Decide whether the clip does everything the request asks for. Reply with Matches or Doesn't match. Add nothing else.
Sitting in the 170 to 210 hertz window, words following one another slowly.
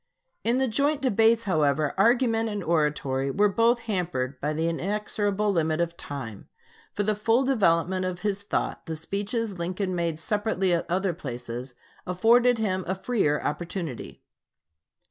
Doesn't match